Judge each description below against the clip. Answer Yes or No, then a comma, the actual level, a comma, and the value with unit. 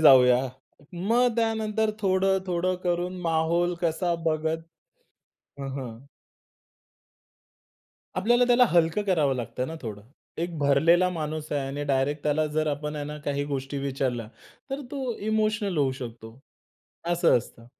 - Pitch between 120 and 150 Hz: No, medium, 160 Hz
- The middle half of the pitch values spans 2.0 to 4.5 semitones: No, average, 4.9 semitones